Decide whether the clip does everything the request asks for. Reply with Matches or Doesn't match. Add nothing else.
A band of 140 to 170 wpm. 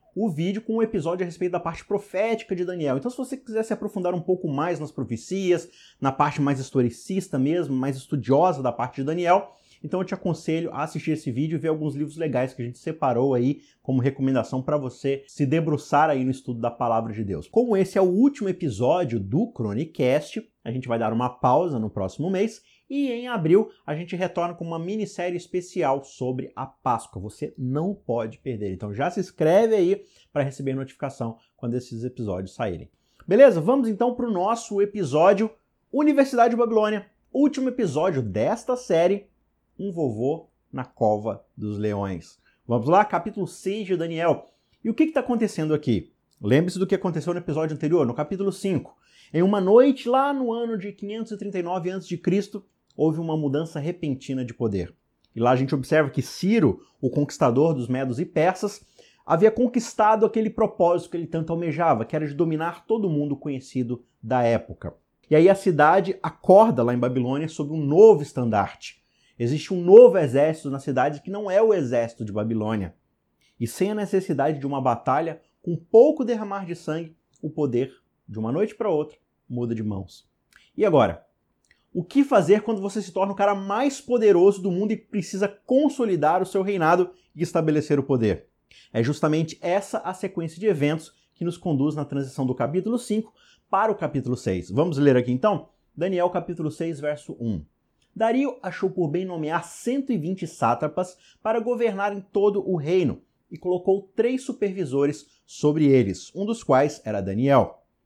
Doesn't match